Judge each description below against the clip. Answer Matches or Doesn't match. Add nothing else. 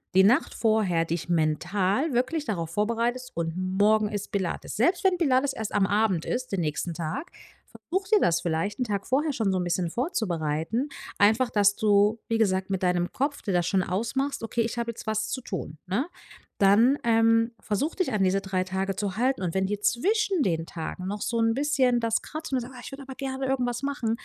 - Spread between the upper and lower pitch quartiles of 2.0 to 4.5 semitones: Doesn't match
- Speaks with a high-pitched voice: Matches